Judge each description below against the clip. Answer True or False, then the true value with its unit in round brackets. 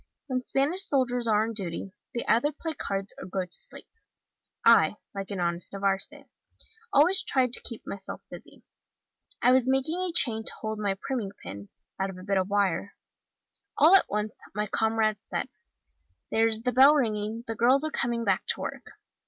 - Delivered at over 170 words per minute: True (180 wpm)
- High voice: True (225 Hz)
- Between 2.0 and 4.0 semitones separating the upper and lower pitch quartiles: False (4.8 semitones)